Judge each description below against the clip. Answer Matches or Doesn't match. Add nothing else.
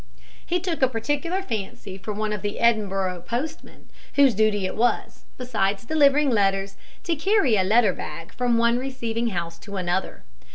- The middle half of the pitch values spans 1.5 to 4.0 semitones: Doesn't match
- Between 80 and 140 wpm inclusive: Doesn't match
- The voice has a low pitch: Doesn't match